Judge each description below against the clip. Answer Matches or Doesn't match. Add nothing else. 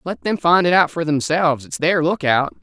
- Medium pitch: Matches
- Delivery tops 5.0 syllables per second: Matches